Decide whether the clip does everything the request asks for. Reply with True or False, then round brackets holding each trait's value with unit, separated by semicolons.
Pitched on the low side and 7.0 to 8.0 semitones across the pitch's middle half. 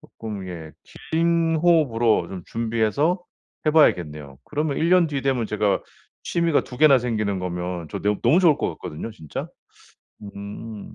True (115 Hz; 7.7 semitones)